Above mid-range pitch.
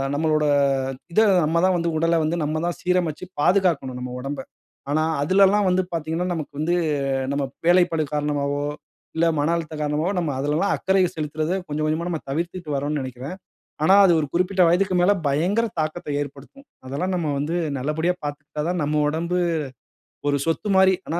No: medium, 160 Hz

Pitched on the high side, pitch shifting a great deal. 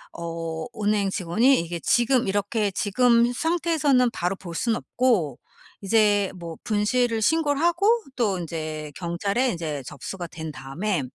Yes: high, 205 Hz; wide, 6.6 semitones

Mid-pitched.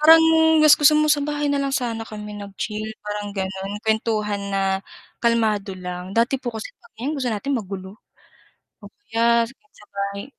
No: high, 220 Hz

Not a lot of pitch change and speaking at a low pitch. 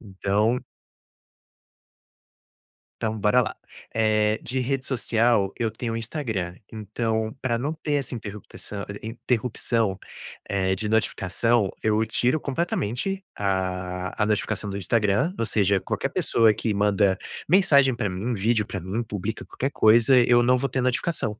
No: average, 3.4 semitones; low, 110 Hz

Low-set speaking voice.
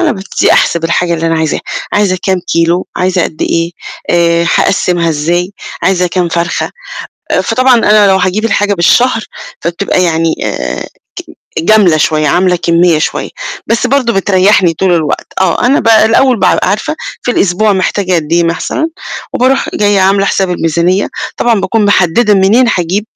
No: medium, 185 Hz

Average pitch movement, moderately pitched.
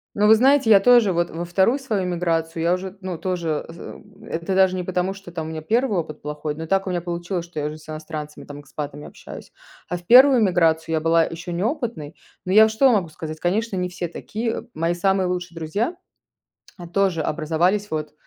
Yes: average, 3.5 semitones; medium, 175 Hz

